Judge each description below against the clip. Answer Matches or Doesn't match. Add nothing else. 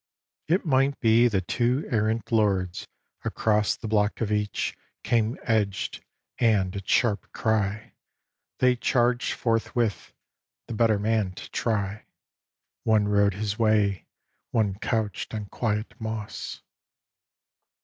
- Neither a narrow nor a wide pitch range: Doesn't match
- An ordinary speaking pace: Doesn't match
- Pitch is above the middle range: Doesn't match